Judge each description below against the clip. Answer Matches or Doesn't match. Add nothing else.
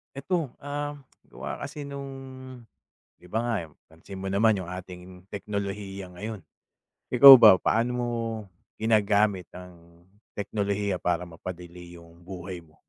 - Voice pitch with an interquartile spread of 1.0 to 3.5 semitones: Doesn't match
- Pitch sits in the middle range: Doesn't match